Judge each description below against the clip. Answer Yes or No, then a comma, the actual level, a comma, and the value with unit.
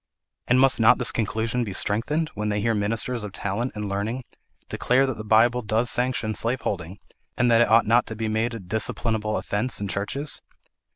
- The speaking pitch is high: No, low, 110 Hz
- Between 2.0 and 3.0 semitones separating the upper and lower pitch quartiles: Yes, average, 2.7 semitones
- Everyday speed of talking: Yes, average, 190 wpm